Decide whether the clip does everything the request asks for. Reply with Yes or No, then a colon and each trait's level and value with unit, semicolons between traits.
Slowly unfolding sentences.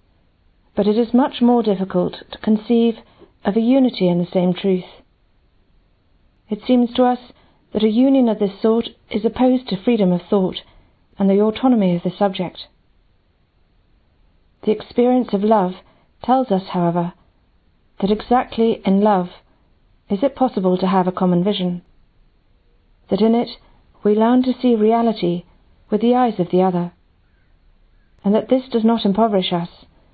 No: average, 155 wpm